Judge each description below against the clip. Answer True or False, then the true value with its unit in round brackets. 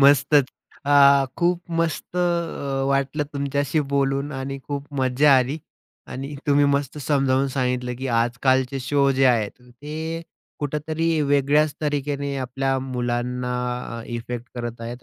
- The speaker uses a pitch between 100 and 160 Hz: True (140 Hz)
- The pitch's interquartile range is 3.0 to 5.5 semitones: False (2.4 semitones)